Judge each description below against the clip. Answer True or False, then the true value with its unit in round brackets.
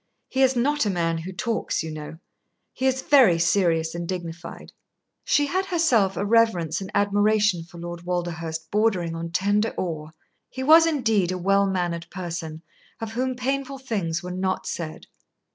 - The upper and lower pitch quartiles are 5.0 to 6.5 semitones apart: True (5.6 semitones)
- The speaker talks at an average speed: True (165 wpm)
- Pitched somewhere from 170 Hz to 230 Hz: True (190 Hz)